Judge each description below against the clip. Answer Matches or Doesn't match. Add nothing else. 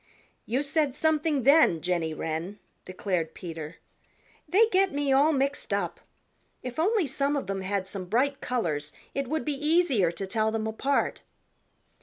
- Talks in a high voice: Matches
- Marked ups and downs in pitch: Matches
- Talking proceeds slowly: Doesn't match